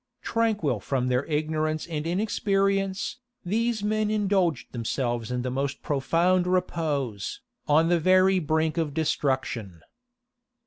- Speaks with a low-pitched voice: No, medium, 160 Hz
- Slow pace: Yes, slow, 120 wpm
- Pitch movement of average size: No, wide, 5.8 semitones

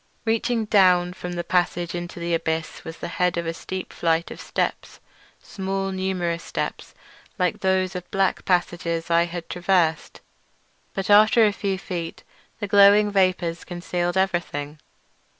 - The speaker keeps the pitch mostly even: Yes, narrow, 2.1 semitones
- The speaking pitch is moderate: Yes, medium, 180 Hz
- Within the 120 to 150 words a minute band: Yes, average, 145 wpm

